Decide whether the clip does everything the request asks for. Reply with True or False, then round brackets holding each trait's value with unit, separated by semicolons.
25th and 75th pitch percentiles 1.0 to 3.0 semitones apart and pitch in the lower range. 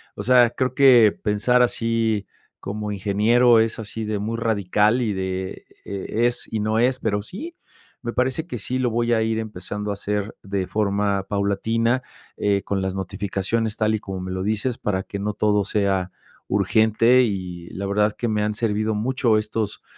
True (2.5 semitones; 105 Hz)